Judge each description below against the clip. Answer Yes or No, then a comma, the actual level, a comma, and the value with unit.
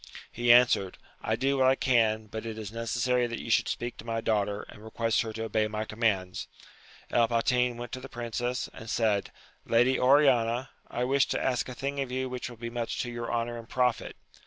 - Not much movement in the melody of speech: Yes, narrow, 1.9 semitones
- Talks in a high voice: No, low, 120 Hz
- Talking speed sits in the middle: No, fast, 215 wpm